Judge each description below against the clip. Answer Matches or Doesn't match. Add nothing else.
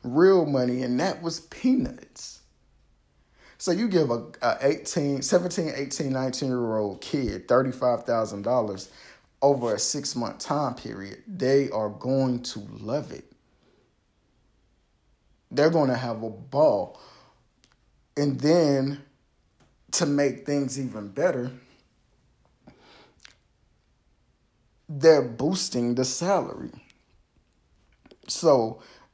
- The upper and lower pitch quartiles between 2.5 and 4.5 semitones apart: Matches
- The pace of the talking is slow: Matches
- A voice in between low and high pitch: Doesn't match